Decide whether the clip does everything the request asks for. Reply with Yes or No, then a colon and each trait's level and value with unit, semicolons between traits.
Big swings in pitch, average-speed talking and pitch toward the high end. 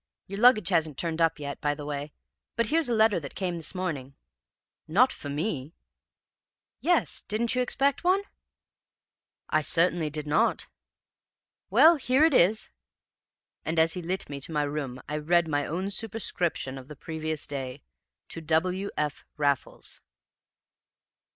No: wide, 5.9 semitones; average, 150 wpm; medium, 165 Hz